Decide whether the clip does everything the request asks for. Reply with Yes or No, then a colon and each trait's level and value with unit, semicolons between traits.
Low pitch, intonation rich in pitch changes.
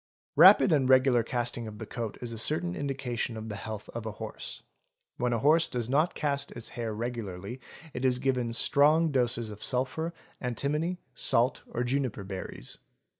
No: low, 125 Hz; average, 3.4 semitones